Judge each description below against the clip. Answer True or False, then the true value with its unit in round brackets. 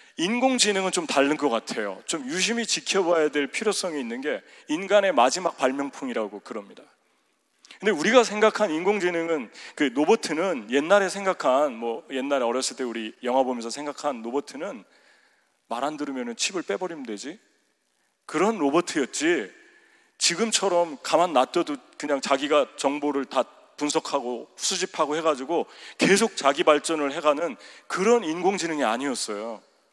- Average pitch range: False (6.8 semitones)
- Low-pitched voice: False (160 Hz)